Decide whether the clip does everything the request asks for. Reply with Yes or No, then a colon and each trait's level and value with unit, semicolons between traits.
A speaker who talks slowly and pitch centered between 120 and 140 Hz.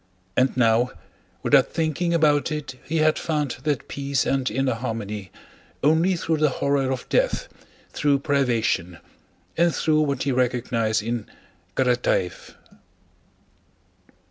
Yes: slow, 120 wpm; low, 135 Hz